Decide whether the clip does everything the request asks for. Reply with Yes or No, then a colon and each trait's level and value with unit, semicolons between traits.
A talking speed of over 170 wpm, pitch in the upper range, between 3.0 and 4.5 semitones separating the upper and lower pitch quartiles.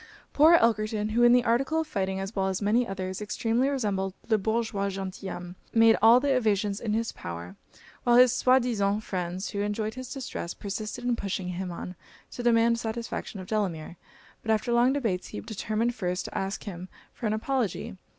Yes: average, 190 wpm; high, 215 Hz; average, 3.7 semitones